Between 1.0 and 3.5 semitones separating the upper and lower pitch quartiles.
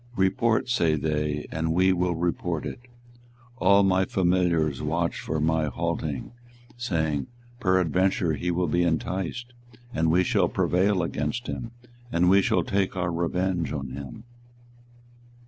Yes: average, 2.8 semitones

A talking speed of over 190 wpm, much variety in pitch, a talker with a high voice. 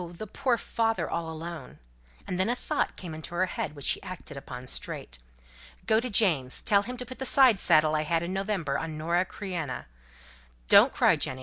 No: average, 200 wpm; wide, 5.8 semitones; medium, 175 Hz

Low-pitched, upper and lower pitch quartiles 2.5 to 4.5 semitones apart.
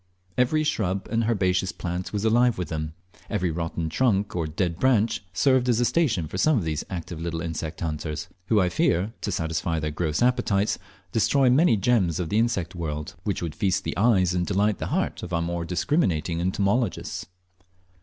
No: very low, 95 Hz; average, 5.3 semitones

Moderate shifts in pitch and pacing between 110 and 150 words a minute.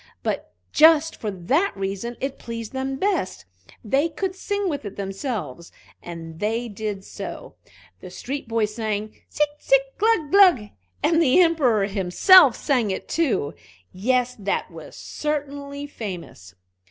No: wide, 7.1 semitones; average, 140 wpm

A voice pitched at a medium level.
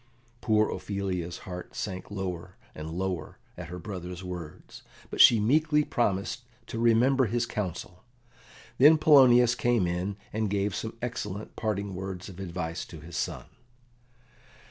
No: low, 100 Hz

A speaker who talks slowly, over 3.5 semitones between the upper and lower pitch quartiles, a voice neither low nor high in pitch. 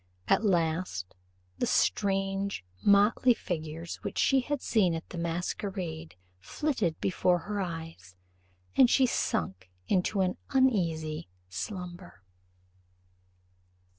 Yes: slow, 105 wpm; average, 3.9 semitones; medium, 180 Hz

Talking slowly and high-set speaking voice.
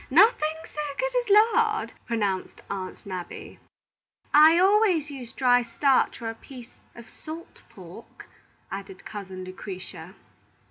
Yes: slow, 125 wpm; very high, 260 Hz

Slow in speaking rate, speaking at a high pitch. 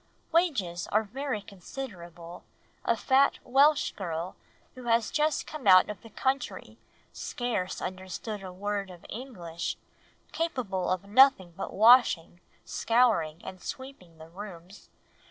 Yes: slow, 125 wpm; high, 205 Hz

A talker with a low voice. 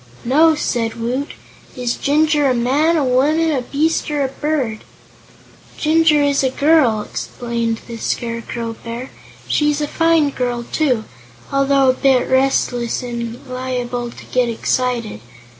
No: very high, 260 Hz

